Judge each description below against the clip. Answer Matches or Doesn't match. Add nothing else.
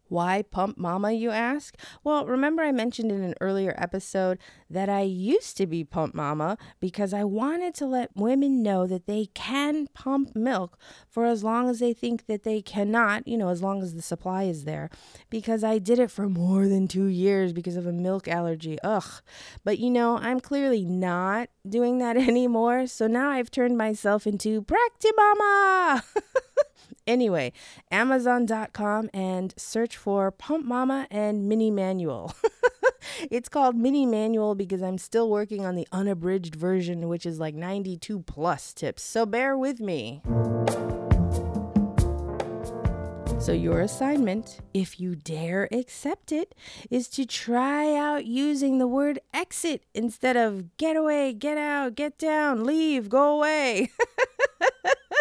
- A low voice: Doesn't match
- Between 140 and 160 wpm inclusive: Matches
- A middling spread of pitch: Doesn't match